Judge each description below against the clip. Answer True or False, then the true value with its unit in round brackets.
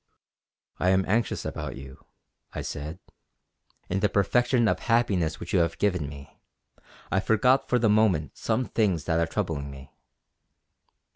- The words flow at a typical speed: True (150 wpm)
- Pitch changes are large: True (6.0 semitones)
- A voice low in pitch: True (95 Hz)